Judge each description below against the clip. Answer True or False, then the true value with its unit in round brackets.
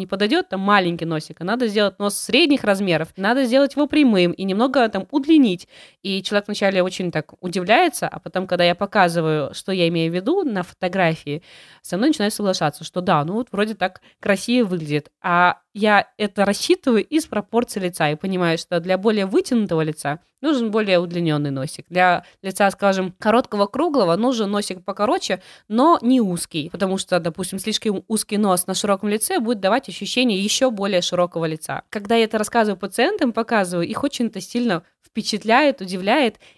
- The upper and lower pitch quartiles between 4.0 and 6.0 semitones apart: True (4.4 semitones)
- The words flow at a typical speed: False (170 wpm)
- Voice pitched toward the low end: False (200 Hz)